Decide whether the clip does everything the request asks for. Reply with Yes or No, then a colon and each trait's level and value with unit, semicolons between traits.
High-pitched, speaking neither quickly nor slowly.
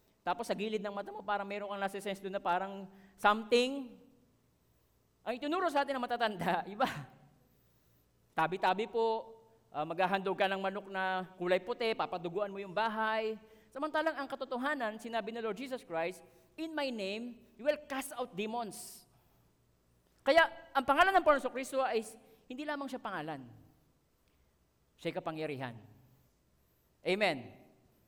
Yes: high, 210 Hz; average, 140 wpm